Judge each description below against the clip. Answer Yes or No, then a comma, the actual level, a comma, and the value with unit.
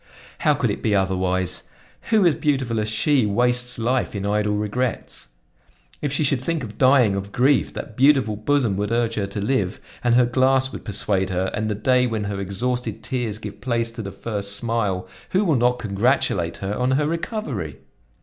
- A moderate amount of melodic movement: Yes, average, 4.2 semitones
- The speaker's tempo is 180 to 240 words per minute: Yes, average, 190 wpm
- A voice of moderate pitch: No, low, 115 Hz